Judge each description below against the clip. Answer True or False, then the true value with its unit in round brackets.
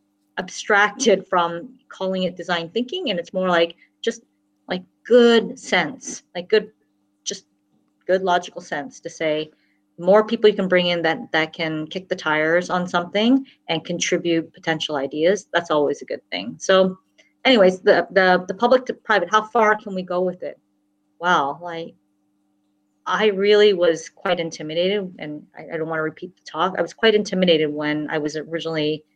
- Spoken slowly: False (175 wpm)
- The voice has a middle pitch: True (175 Hz)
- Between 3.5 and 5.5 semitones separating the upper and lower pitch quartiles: True (4.1 semitones)